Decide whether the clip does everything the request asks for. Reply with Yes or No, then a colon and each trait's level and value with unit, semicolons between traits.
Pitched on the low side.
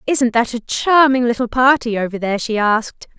No: high, 240 Hz